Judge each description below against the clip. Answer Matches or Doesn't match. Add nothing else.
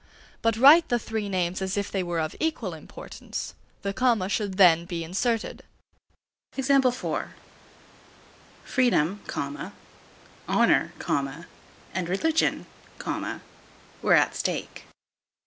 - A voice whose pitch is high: Matches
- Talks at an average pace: Doesn't match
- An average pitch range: Doesn't match